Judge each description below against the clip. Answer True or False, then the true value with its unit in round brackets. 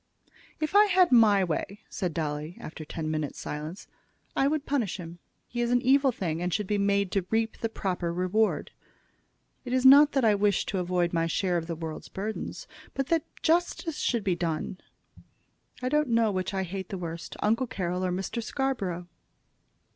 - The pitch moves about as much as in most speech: False (6.0 semitones)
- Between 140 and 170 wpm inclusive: False (185 wpm)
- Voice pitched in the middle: False (200 Hz)